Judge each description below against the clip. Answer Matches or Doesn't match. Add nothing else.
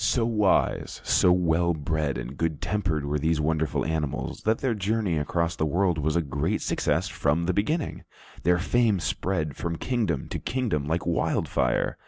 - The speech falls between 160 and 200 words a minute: Matches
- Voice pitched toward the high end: Doesn't match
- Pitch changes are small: Doesn't match